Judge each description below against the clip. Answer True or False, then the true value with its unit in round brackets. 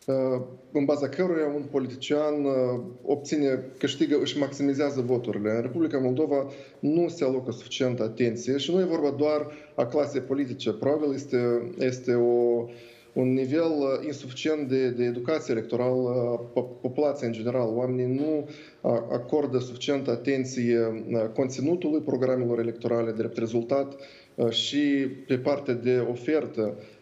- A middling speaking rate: True (125 wpm)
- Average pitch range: True (3.0 semitones)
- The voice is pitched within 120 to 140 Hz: True (130 Hz)